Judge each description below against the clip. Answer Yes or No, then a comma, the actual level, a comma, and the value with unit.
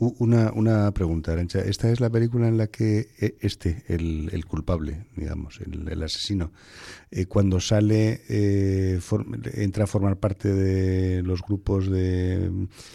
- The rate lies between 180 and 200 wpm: No, average, 150 wpm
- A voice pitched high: No, low, 100 Hz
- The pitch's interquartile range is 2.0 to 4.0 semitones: Yes, average, 2.8 semitones